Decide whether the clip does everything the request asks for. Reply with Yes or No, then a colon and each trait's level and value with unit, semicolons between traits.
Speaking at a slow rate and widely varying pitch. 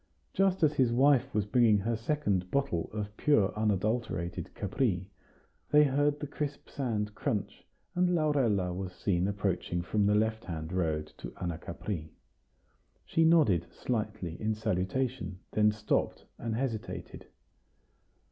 Yes: slow, 130 wpm; wide, 6.2 semitones